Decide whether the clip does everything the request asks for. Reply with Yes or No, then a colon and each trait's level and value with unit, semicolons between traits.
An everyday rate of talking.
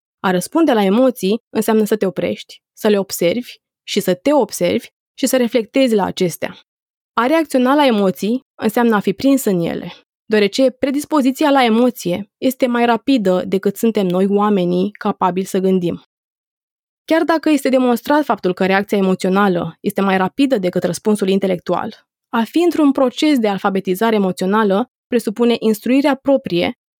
Yes: average, 150 wpm